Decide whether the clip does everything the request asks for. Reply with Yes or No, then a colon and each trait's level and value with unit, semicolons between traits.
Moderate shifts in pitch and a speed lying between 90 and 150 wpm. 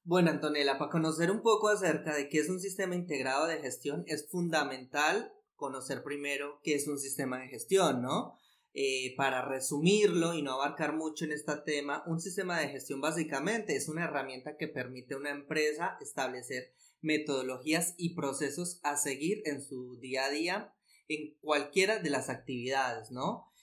No: average, 3.4 semitones; average, 170 wpm